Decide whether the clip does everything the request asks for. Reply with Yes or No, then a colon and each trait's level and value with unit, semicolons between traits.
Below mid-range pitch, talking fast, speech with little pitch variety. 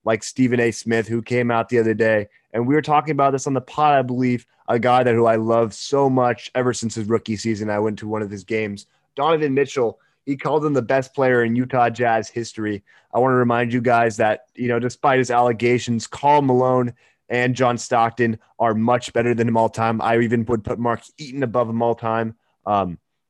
Yes: low, 120 Hz; fast, 225 wpm; narrow, 1.9 semitones